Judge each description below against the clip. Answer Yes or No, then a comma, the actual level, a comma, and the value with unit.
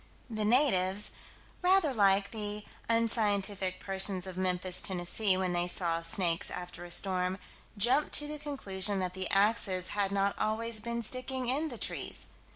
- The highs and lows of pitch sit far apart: No, average, 3.8 semitones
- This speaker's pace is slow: No, average, 155 wpm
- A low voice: No, high, 200 Hz